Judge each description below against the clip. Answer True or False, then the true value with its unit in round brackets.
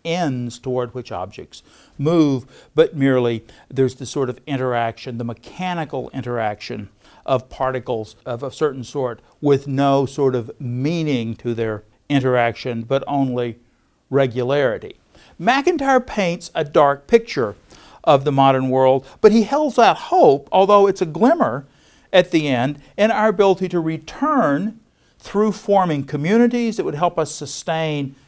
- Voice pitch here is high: False (140 Hz)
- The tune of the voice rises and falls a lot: True (6.4 semitones)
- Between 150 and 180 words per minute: False (140 wpm)